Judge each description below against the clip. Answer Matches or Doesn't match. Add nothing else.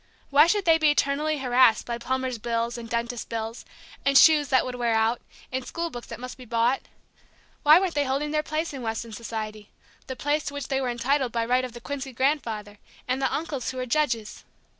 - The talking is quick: Matches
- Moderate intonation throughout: Matches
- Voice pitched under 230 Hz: Doesn't match